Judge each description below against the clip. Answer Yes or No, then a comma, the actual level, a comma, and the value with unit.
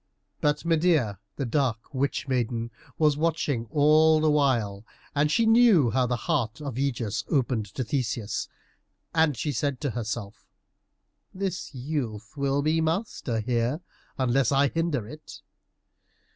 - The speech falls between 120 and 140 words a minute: Yes, slow, 135 wpm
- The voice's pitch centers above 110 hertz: Yes, medium, 140 Hz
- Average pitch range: Yes, average, 4.5 semitones